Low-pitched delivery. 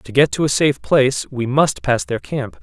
Yes: low, 130 Hz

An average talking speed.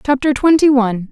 Yes: average, 160 wpm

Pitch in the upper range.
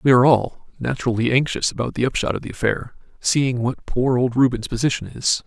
No: low, 125 Hz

